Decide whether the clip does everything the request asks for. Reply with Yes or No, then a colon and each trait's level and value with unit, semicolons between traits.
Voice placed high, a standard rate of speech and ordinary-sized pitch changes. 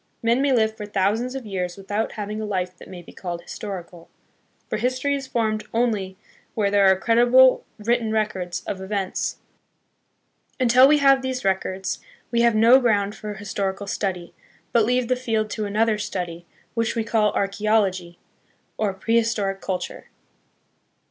Yes: high, 215 Hz; average, 160 wpm; average, 3.4 semitones